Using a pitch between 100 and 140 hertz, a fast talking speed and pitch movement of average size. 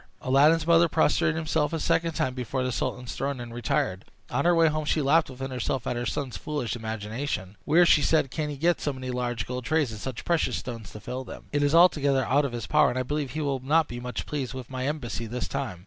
Yes: low, 135 Hz; fast, 245 wpm; average, 3.8 semitones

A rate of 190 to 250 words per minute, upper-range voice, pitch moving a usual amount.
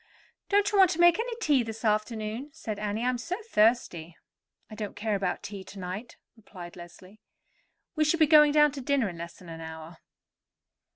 No: average, 195 wpm; high, 220 Hz; wide, 7.7 semitones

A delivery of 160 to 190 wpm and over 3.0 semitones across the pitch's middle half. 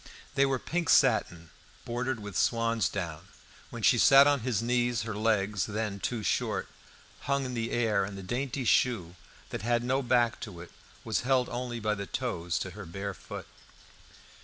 Yes: average, 175 wpm; average, 4.0 semitones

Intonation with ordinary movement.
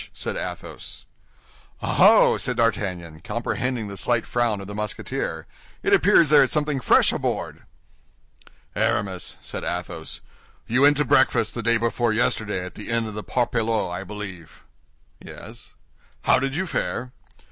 Yes: average, 3.8 semitones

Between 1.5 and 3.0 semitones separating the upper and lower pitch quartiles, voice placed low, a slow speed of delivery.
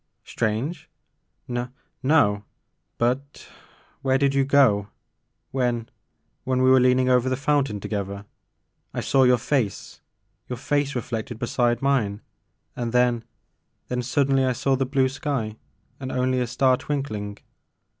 No: narrow, 2.6 semitones; low, 125 Hz; average, 150 wpm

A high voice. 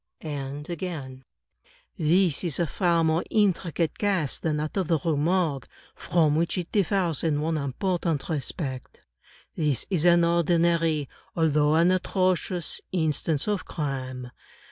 No: medium, 165 Hz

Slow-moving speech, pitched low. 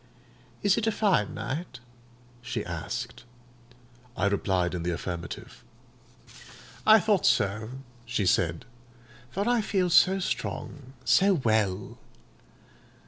Yes: slow, 110 wpm; low, 120 Hz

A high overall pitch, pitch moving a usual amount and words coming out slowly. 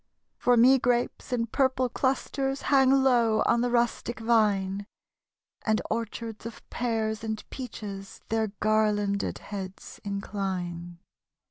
Yes: high, 225 Hz; average, 3.3 semitones; slow, 115 wpm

